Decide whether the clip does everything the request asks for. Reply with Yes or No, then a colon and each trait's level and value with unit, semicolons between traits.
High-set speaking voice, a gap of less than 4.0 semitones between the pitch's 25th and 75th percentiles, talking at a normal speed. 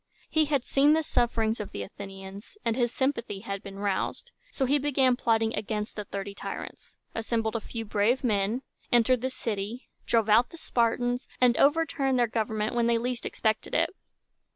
Yes: high, 230 Hz; average, 3.3 semitones; average, 175 wpm